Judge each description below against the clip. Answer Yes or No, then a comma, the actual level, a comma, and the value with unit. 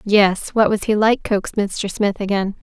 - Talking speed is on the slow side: No, average, 200 wpm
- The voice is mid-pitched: No, high, 205 Hz